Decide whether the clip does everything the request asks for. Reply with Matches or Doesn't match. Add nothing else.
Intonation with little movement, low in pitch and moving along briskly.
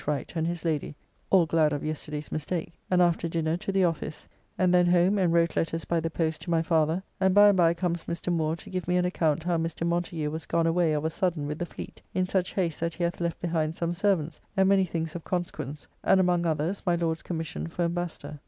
Doesn't match